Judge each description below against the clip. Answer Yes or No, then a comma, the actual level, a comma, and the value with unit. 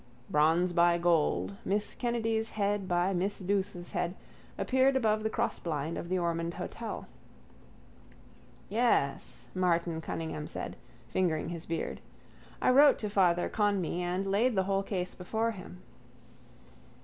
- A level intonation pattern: No, average, 3.5 semitones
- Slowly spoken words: Yes, slow, 130 wpm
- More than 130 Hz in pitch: Yes, medium, 185 Hz